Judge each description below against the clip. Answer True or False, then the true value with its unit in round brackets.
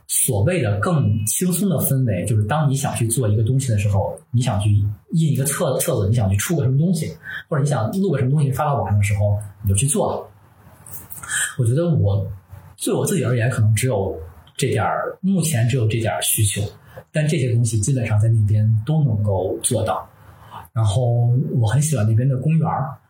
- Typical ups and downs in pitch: True (4.9 semitones)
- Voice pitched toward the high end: False (120 Hz)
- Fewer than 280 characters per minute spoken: False (295 characters per minute)